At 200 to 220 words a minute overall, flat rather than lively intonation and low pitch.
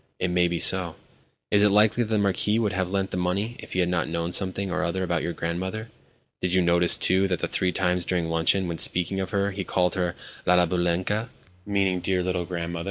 Yes: fast, 205 wpm; narrow, 2.1 semitones; very low, 90 Hz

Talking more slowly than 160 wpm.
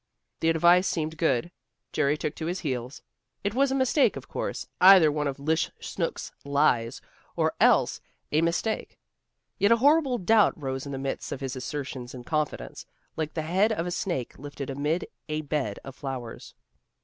No: average, 175 wpm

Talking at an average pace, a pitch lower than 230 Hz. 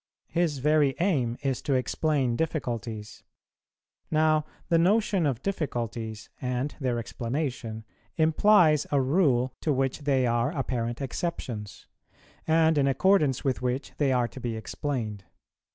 No: slow, 130 wpm; low, 135 Hz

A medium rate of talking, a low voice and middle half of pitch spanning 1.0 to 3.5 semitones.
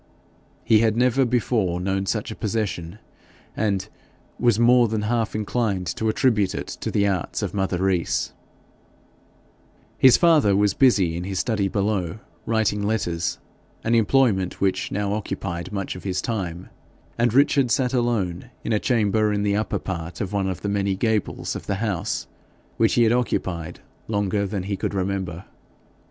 Yes: average, 165 wpm; low, 105 Hz; average, 3.1 semitones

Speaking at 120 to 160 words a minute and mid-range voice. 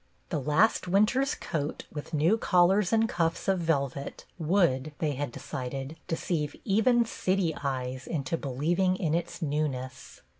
Yes: average, 145 wpm; medium, 160 Hz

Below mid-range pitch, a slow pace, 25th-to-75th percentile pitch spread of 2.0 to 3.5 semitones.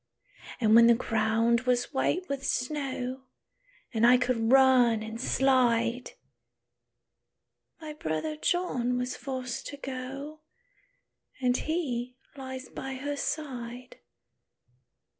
No: very high, 255 Hz; slow, 105 wpm; narrow, 2.5 semitones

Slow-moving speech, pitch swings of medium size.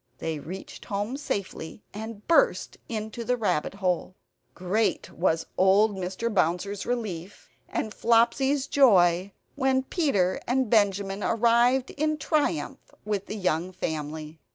Yes: slow, 125 wpm; average, 4.6 semitones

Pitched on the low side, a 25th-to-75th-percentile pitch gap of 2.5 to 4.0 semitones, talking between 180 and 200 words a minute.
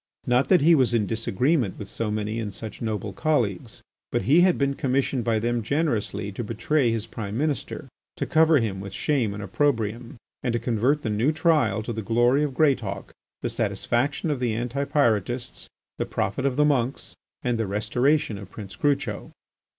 No: low, 120 Hz; average, 4.8 semitones; average, 185 wpm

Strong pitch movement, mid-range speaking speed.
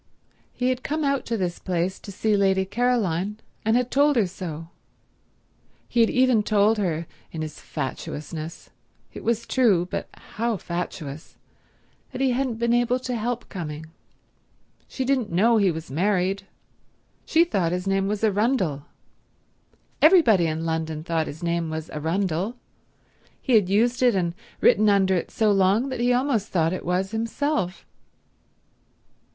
Yes: wide, 5.7 semitones; average, 150 wpm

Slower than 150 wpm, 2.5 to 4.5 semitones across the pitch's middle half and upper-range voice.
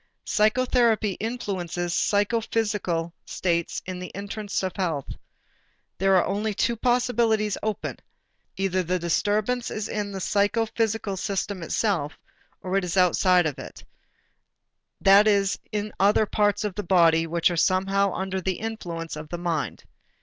Yes: average, 140 wpm; average, 3.1 semitones; high, 195 Hz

